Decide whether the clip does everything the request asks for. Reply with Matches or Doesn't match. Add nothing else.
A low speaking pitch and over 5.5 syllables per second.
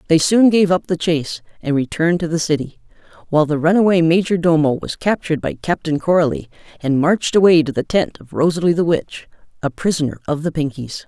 Doesn't match